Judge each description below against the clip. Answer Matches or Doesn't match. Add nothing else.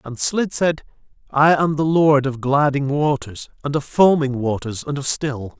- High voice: Doesn't match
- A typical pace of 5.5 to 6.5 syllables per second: Doesn't match